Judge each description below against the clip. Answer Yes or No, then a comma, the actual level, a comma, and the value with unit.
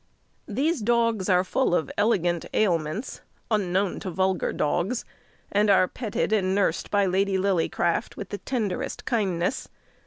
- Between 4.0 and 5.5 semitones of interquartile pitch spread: No, average, 3.2 semitones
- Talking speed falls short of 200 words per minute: Yes, slow, 135 wpm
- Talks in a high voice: Yes, high, 195 Hz